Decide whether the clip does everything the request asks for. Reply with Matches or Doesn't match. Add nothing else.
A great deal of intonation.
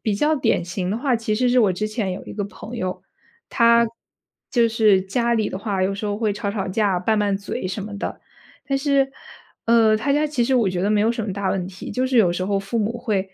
Doesn't match